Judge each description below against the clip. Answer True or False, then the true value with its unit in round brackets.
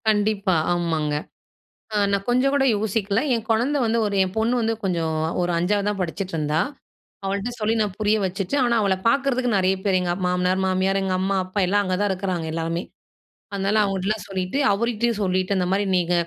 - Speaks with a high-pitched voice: True (195 Hz)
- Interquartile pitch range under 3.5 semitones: True (2.8 semitones)